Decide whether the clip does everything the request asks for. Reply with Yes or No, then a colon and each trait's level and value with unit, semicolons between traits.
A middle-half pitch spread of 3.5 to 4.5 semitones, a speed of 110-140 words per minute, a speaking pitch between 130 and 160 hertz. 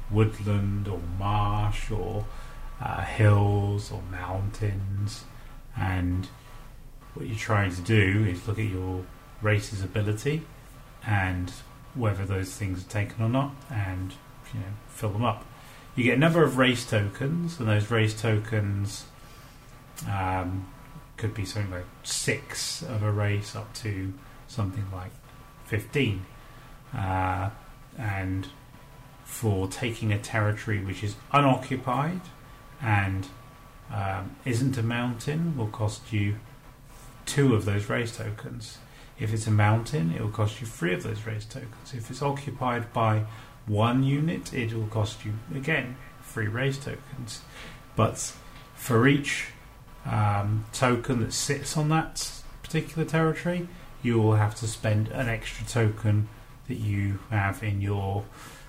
No: average, 4.0 semitones; slow, 135 wpm; low, 115 Hz